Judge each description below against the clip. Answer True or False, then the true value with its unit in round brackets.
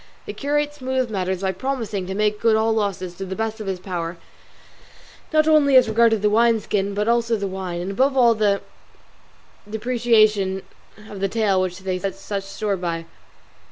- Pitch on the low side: False (210 Hz)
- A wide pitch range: False (3.4 semitones)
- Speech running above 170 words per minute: True (185 wpm)